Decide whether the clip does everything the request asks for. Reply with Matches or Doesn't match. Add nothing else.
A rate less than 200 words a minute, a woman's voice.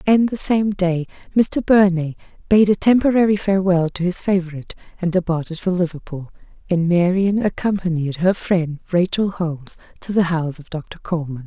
Matches